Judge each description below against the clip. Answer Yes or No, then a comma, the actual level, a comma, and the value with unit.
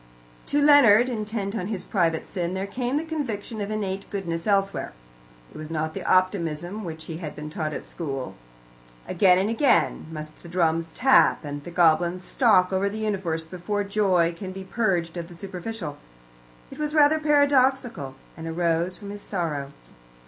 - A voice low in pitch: No, medium, 185 Hz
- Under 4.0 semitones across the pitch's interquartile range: No, average, 4.5 semitones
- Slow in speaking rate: No, average, 170 wpm